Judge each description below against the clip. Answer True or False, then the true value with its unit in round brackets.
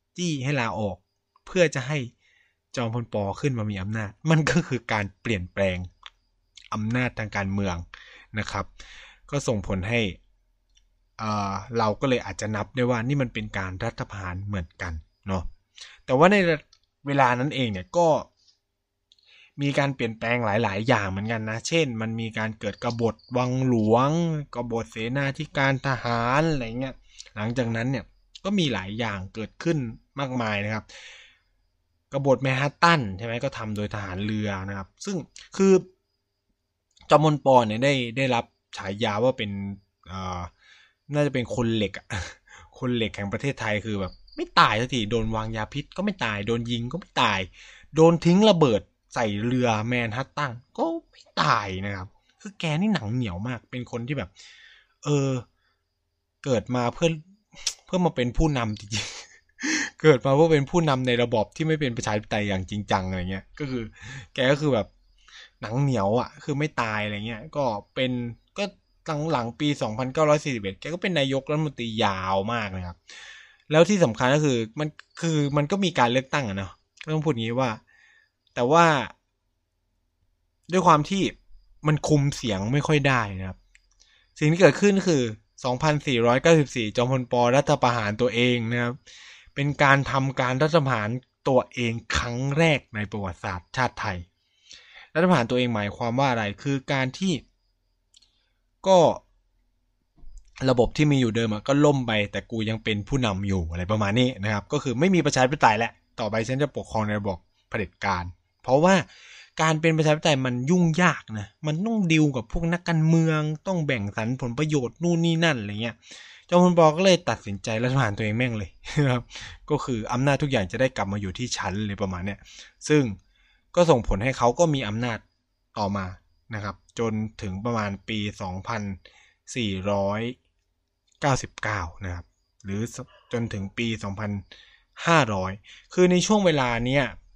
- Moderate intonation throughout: False (6.0 semitones)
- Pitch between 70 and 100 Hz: False (120 Hz)